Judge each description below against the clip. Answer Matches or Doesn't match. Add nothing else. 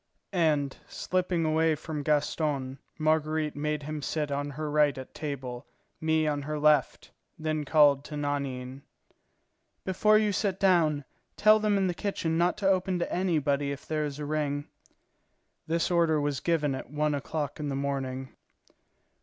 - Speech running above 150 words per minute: Matches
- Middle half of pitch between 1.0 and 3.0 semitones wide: Matches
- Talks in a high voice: Doesn't match